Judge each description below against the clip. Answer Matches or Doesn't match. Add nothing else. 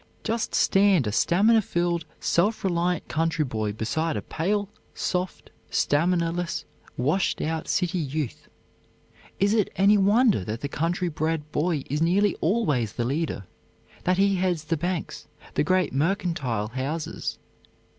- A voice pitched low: Doesn't match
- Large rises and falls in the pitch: Doesn't match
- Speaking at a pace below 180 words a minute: Matches